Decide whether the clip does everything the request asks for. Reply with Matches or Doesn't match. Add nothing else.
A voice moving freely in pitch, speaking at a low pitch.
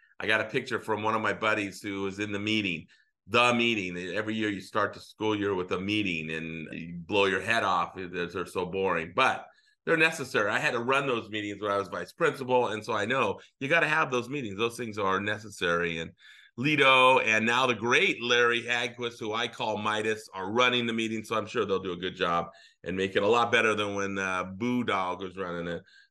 Doesn't match